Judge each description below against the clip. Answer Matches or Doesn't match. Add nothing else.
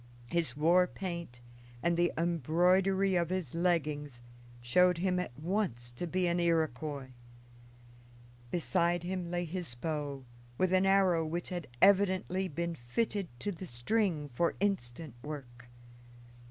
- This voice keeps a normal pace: Doesn't match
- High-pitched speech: Doesn't match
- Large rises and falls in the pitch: Doesn't match